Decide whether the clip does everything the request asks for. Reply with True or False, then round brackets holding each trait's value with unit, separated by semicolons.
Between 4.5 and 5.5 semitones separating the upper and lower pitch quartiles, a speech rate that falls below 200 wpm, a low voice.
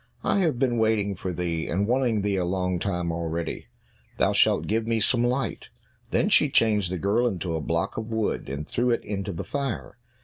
False (4.9 semitones; 205 wpm; 100 Hz)